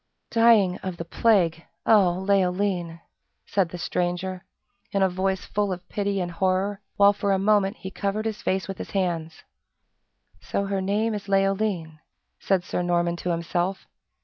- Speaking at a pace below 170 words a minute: Yes, average, 160 wpm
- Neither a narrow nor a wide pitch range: No, narrow, 2.2 semitones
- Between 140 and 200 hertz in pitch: Yes, high, 190 Hz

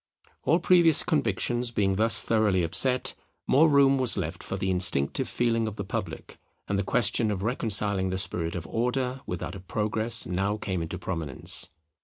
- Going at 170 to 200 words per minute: Yes, average, 175 wpm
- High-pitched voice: No, low, 105 Hz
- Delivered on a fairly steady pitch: No, average, 4.6 semitones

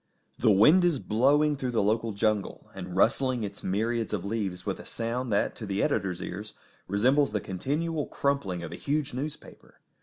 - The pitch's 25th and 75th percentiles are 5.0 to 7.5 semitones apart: Yes, wide, 5.4 semitones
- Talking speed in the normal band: Yes, average, 180 wpm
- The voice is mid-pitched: No, low, 115 Hz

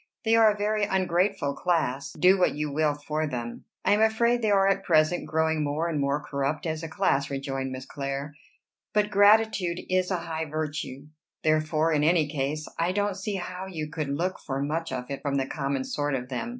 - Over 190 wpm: Yes, fast, 205 wpm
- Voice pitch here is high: No, medium, 155 Hz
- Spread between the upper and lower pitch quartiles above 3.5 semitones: Yes, average, 4.7 semitones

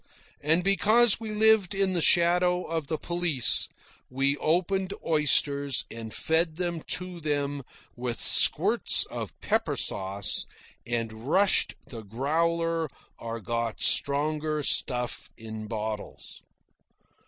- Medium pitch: Yes, medium, 155 Hz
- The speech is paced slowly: Yes, slow, 115 wpm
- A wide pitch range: Yes, wide, 6.6 semitones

